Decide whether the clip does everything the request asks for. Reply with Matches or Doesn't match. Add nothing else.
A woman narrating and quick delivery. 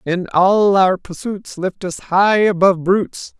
Doesn't match